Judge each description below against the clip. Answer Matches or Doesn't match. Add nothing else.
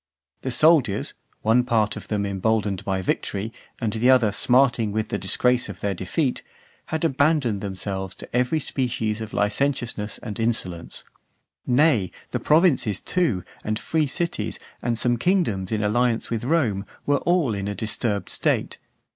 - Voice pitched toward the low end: Matches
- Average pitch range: Matches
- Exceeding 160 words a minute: Doesn't match